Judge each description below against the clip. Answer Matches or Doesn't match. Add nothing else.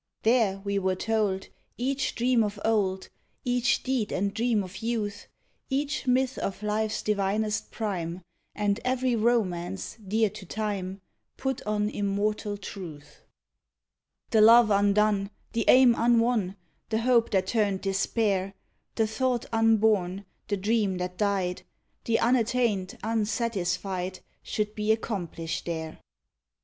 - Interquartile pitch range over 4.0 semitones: Doesn't match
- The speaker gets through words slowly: Matches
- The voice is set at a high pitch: Matches